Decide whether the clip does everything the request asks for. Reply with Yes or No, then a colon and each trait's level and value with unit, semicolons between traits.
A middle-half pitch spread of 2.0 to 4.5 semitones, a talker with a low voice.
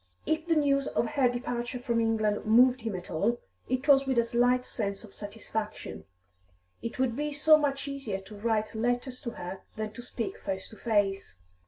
No: average, 3.6 semitones; high, 235 Hz